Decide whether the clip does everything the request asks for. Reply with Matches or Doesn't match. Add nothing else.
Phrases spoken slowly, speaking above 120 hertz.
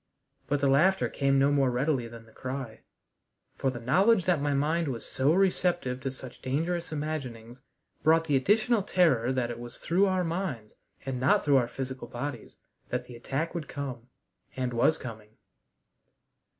Doesn't match